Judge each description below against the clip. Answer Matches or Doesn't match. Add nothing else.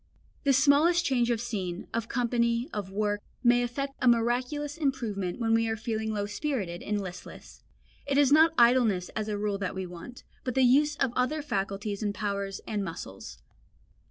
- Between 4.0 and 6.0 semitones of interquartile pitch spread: Matches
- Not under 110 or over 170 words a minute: Doesn't match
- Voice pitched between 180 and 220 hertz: Doesn't match